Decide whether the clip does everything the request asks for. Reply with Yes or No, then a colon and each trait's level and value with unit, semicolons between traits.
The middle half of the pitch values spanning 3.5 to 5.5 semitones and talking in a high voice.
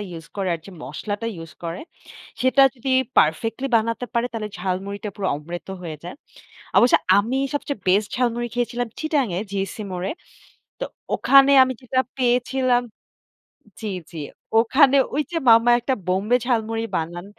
Yes: average, 4.8 semitones; high, 225 Hz